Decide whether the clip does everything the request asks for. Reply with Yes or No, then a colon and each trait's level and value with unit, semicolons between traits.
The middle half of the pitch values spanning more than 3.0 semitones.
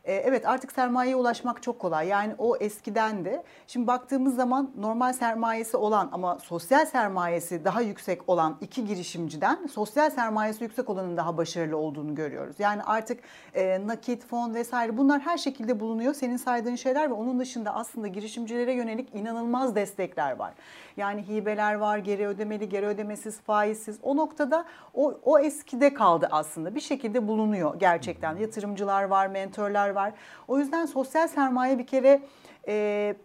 Yes: average, 3.9 semitones